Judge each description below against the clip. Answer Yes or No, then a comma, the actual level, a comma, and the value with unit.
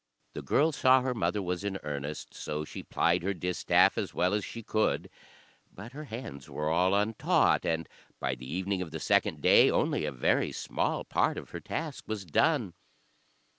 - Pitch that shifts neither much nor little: No, wide, 6.0 semitones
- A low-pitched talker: Yes, very low, 95 Hz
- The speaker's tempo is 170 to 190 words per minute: Yes, average, 185 wpm